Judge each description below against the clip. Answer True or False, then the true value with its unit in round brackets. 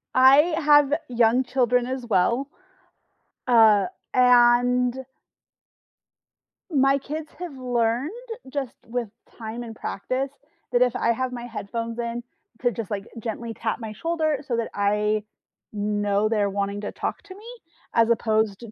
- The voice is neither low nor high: False (240 Hz)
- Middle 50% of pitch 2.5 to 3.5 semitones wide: True (2.9 semitones)